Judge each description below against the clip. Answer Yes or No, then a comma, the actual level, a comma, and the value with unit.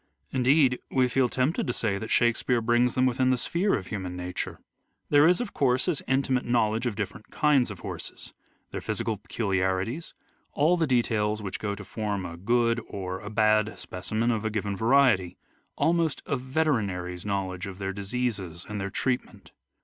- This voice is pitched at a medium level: No, low, 110 Hz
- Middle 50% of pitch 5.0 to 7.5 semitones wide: No, average, 4.6 semitones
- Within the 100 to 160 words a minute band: No, average, 175 wpm